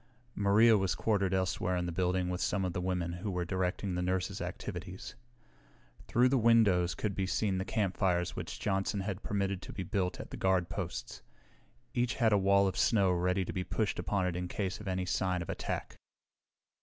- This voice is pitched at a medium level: No, very low, 95 Hz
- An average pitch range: No, narrow, 1.8 semitones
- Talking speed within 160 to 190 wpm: No, average, 200 wpm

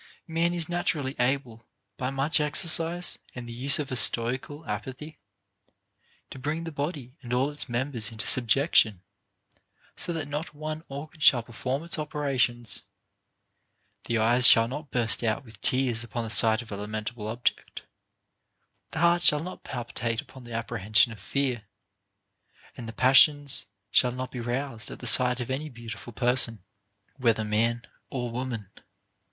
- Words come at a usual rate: Yes, average, 160 wpm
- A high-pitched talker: No, low, 125 Hz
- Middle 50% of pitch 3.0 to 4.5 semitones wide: Yes, average, 3.9 semitones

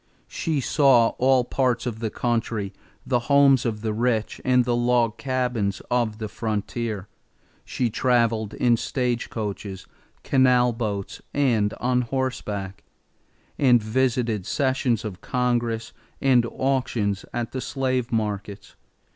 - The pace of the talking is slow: Yes, slow, 120 wpm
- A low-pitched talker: Yes, low, 120 Hz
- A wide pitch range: No, average, 2.7 semitones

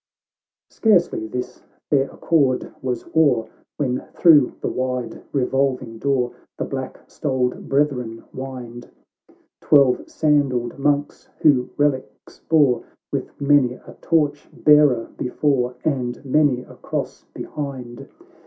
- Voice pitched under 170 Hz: Yes, low, 135 Hz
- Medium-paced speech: No, slow, 115 wpm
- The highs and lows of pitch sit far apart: No, average, 2.8 semitones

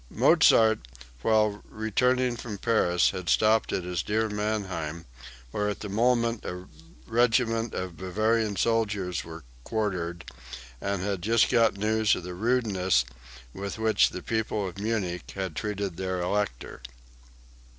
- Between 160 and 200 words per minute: No, slow, 135 wpm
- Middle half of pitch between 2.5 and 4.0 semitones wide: Yes, average, 3.4 semitones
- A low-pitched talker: Yes, low, 105 Hz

